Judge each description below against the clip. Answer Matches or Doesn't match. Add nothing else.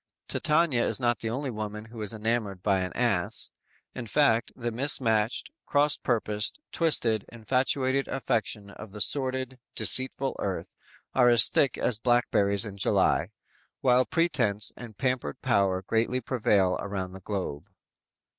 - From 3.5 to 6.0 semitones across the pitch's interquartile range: Matches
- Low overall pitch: Matches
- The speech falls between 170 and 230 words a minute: Doesn't match